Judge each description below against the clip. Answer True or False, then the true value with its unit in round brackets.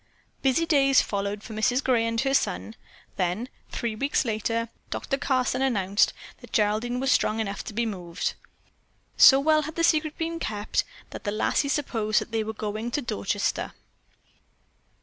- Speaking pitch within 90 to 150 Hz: False (230 Hz)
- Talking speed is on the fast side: False (165 wpm)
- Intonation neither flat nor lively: True (4.3 semitones)